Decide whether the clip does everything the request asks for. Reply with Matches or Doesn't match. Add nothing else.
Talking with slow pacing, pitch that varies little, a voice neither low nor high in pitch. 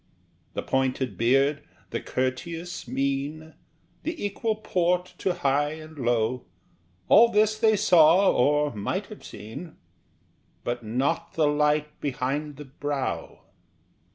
Doesn't match